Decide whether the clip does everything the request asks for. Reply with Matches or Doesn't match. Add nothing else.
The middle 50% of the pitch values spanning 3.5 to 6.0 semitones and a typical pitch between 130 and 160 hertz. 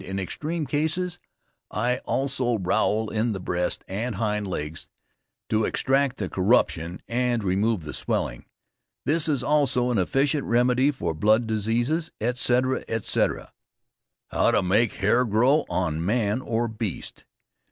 Doesn't match